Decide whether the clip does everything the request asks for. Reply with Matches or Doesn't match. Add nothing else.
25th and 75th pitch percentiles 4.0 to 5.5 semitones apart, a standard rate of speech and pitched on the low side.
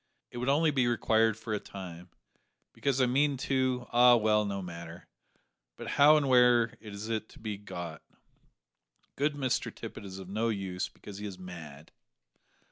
Matches